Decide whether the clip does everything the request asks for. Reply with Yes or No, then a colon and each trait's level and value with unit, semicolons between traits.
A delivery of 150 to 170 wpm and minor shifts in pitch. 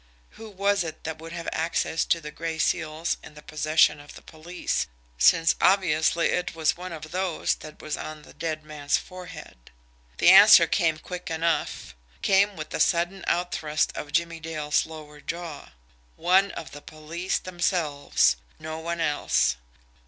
Yes: average, 165 wpm; narrow, 2.2 semitones